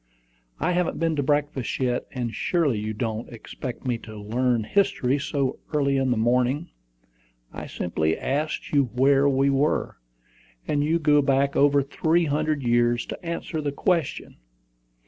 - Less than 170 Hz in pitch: Yes, medium, 140 Hz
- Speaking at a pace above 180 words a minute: No, average, 155 wpm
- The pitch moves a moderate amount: Yes, average, 3.5 semitones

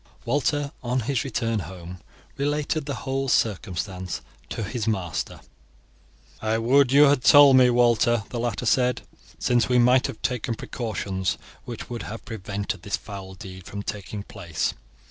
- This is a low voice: Yes, low, 115 Hz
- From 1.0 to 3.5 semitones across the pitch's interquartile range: No, average, 4.3 semitones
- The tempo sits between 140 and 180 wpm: Yes, average, 150 wpm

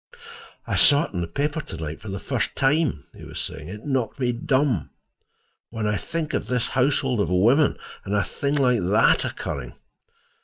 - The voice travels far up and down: Yes, wide, 6.3 semitones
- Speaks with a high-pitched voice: No, low, 120 Hz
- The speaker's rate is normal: Yes, average, 190 wpm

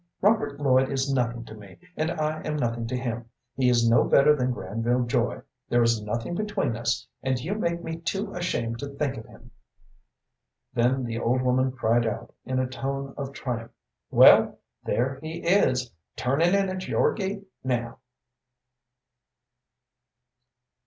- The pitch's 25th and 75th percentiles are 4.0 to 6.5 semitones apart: Yes, average, 4.5 semitones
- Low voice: Yes, low, 130 Hz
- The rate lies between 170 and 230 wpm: No, average, 160 wpm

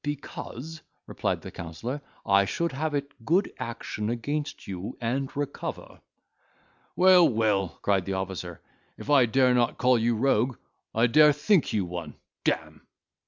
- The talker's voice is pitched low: Yes, low, 120 Hz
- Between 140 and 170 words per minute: Yes, average, 145 wpm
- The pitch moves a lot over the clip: Yes, wide, 6.1 semitones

